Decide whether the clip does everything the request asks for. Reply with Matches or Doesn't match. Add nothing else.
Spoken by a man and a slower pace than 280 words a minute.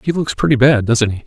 Doesn't match